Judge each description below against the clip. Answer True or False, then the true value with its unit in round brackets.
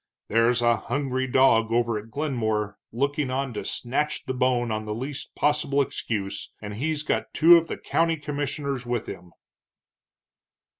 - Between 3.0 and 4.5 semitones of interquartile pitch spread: True (4.1 semitones)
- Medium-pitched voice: False (130 Hz)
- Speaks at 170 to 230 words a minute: False (155 wpm)